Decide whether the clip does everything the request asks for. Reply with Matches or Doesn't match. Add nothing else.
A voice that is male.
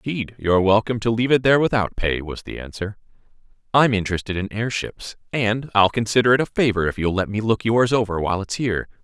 Matches